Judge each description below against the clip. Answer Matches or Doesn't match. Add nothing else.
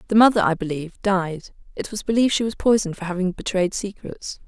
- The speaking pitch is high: Matches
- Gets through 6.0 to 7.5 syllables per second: Matches